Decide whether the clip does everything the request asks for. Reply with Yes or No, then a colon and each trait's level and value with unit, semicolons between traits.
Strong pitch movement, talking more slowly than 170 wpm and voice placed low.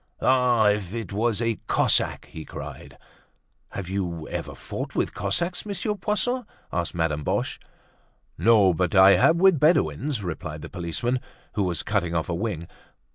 Yes: wide, 6.8 semitones; average, 155 wpm; low, 100 Hz